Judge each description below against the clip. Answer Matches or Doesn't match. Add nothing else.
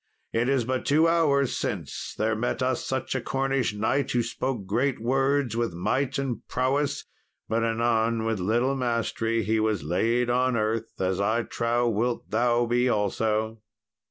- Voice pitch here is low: Matches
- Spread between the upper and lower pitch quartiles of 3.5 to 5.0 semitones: Doesn't match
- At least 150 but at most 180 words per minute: Matches